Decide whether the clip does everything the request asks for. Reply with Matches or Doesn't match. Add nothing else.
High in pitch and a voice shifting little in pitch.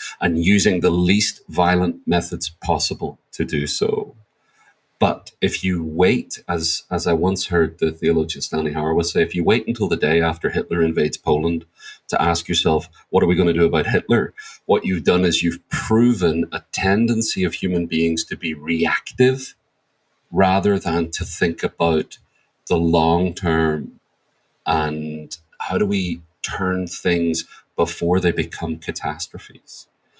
Doesn't match